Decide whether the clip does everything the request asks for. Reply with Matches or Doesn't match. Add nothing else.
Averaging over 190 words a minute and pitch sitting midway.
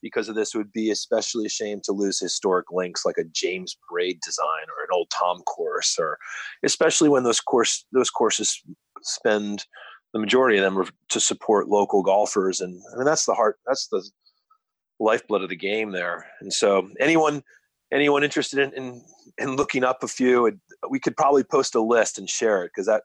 Matches